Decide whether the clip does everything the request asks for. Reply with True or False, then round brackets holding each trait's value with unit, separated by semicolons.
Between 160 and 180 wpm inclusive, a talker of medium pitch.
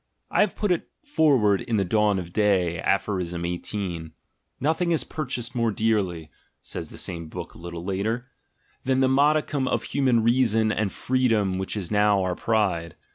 False (170 wpm; 105 Hz)